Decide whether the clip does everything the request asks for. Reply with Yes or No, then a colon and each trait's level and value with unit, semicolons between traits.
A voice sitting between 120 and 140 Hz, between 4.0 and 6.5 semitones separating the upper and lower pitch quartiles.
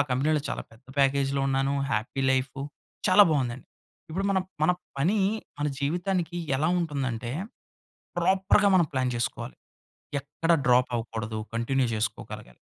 Yes: low, 135 Hz; average, 4.9 semitones